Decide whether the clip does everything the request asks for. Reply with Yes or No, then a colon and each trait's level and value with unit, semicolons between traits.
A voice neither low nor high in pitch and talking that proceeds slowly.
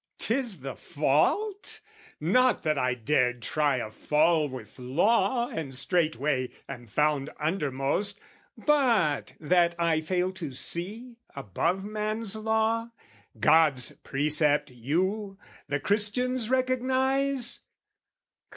Yes: medium, 170 Hz; slow, 105 wpm